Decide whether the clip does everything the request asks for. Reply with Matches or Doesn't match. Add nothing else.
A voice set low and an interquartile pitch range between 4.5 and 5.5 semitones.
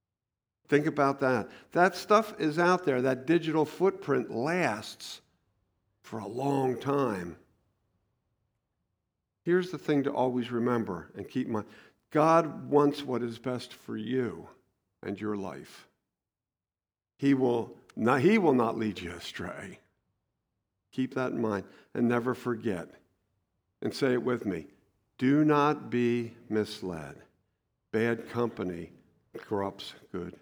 Matches